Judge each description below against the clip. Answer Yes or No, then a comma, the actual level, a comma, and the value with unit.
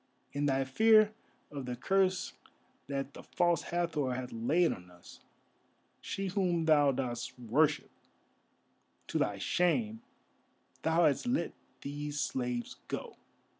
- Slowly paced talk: Yes, slow, 125 wpm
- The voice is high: No, medium, 145 Hz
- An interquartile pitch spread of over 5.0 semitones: Yes, wide, 5.5 semitones